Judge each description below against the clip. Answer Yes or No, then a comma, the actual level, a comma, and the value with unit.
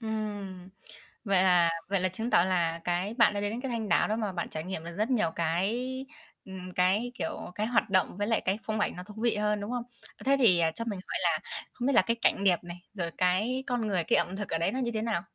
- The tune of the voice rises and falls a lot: No, average, 4.0 semitones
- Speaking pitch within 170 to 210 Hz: Yes, high, 200 Hz